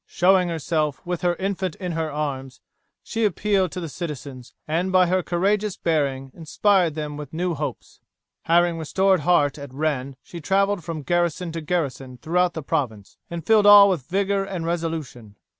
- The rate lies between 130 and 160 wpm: No, average, 170 wpm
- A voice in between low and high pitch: Yes, medium, 165 Hz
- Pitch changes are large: No, average, 3.8 semitones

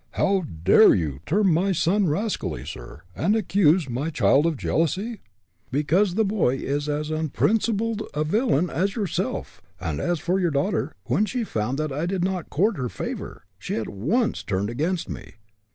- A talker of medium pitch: Yes, medium, 165 Hz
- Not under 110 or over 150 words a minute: No, average, 170 wpm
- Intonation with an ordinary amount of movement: No, wide, 5.8 semitones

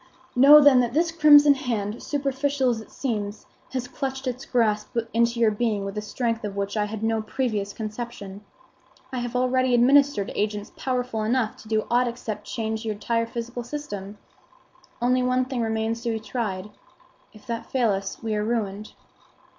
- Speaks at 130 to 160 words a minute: No, average, 180 wpm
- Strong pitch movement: No, average, 3.1 semitones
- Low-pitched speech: No, high, 235 Hz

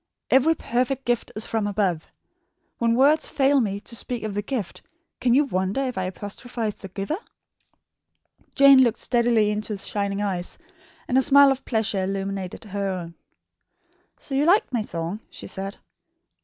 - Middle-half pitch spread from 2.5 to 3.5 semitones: No, average, 4.9 semitones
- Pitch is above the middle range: Yes, high, 220 Hz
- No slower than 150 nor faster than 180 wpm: Yes, average, 165 wpm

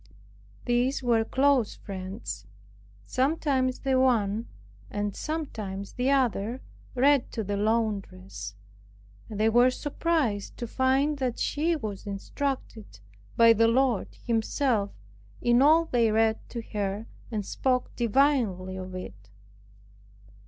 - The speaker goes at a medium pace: No, slow, 115 wpm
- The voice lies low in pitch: No, high, 230 Hz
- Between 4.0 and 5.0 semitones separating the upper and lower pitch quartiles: Yes, average, 4.5 semitones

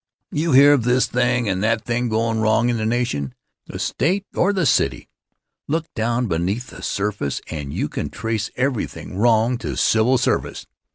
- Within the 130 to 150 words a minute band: No, average, 175 wpm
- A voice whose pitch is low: Yes, low, 115 Hz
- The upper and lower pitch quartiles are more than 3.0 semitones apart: No, narrow, 2.5 semitones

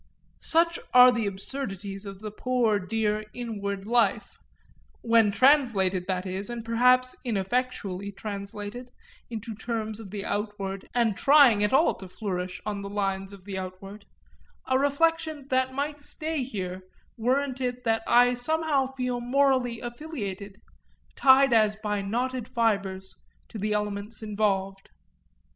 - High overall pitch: Yes, high, 220 Hz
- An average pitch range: Yes, average, 4.1 semitones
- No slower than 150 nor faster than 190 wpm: No, average, 140 wpm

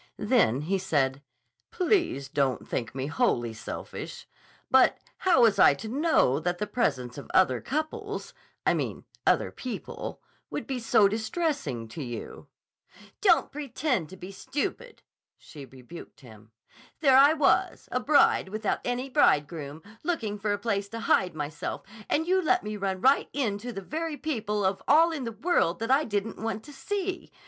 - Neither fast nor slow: Yes, average, 160 wpm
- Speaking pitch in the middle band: No, high, 215 Hz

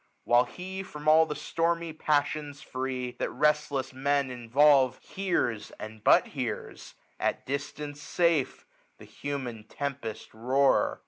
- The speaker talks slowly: Yes, slow, 125 wpm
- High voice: No, medium, 140 Hz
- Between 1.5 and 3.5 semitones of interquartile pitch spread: Yes, average, 2.9 semitones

